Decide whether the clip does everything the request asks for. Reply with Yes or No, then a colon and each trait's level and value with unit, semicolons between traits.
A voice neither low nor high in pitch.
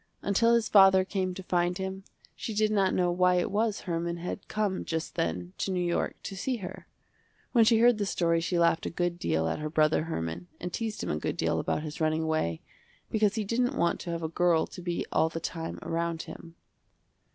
Yes: medium, 175 Hz